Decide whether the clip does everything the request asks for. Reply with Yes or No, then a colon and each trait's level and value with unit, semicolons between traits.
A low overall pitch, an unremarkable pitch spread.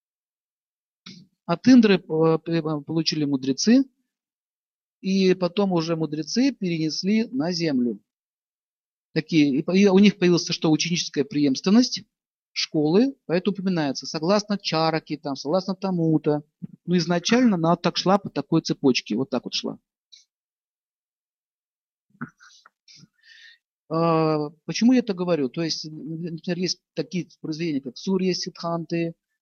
No: medium, 170 Hz; average, 3.5 semitones